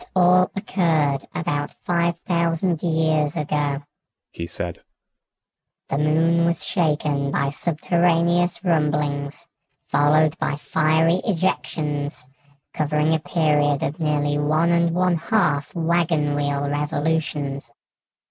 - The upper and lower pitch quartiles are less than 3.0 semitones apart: Yes, narrow, 2.6 semitones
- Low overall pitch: No, medium, 155 Hz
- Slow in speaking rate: Yes, slow, 110 wpm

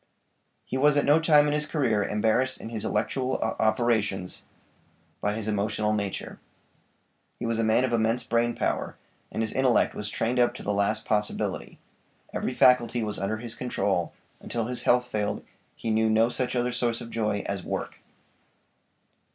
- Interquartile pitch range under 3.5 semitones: Yes, narrow, 2.6 semitones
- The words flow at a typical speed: Yes, average, 170 wpm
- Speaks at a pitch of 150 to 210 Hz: No, low, 115 Hz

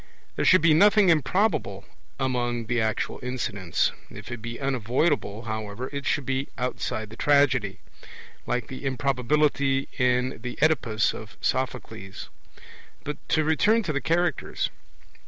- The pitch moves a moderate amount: Yes, average, 4.3 semitones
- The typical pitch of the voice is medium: No, low, 130 Hz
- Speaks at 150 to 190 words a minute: No, slow, 135 wpm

